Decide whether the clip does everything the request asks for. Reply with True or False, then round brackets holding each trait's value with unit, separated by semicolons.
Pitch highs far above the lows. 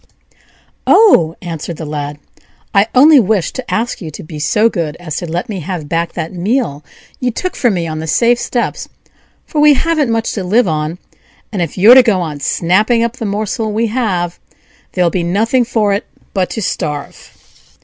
True (5.8 semitones)